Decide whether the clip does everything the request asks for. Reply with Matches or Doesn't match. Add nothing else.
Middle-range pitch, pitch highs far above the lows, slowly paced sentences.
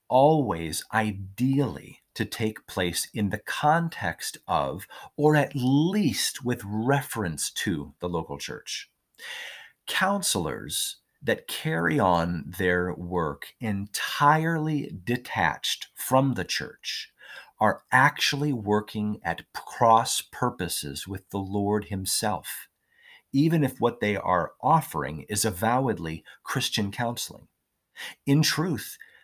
Doesn't match